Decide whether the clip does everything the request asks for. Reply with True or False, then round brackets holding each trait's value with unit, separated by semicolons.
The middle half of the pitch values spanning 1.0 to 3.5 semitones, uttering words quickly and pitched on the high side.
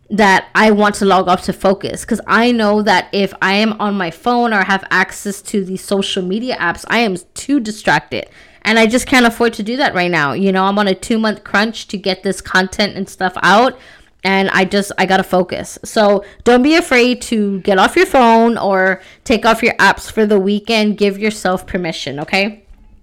True (3.1 semitones; 215 wpm; 200 Hz)